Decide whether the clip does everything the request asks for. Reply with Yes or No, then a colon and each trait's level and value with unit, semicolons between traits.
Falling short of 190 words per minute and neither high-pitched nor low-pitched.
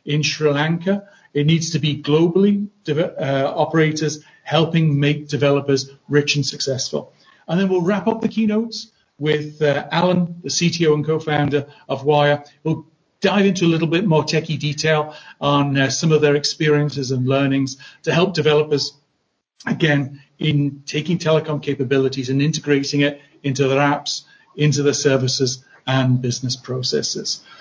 Yes: average, 150 wpm; medium, 150 Hz